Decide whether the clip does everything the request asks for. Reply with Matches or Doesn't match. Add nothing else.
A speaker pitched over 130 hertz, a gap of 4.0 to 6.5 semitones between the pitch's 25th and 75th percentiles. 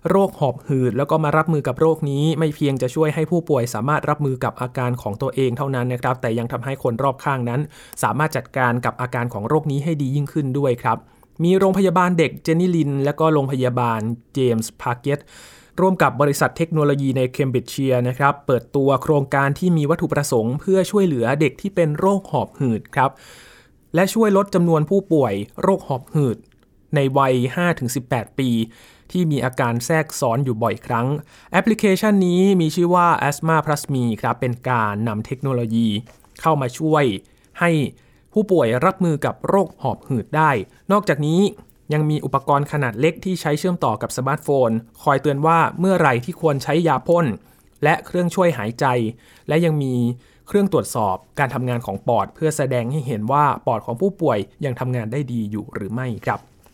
Matches